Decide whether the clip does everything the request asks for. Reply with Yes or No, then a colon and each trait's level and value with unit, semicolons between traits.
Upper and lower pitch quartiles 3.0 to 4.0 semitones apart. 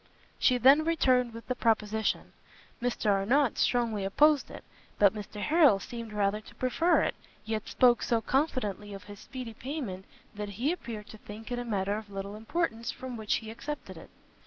Yes: average, 3.6 semitones